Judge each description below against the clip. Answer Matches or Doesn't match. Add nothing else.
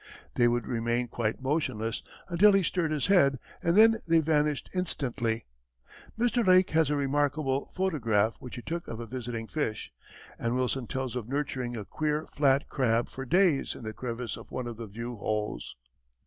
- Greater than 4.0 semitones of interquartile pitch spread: Matches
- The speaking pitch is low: Matches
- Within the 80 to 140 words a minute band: Doesn't match